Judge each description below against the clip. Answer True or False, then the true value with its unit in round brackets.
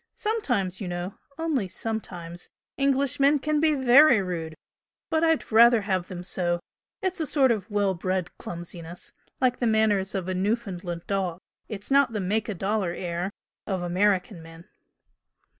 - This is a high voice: True (200 Hz)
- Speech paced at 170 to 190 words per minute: False (155 wpm)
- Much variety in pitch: True (5.7 semitones)